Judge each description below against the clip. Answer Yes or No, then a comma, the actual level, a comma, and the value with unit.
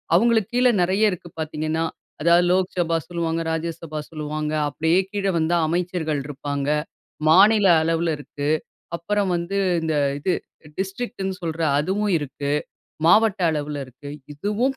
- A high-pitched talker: No, medium, 170 Hz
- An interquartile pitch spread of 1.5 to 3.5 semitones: No, average, 3.9 semitones